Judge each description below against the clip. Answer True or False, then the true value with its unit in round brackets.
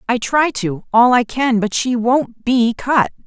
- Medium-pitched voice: False (240 Hz)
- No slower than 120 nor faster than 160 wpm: False (200 wpm)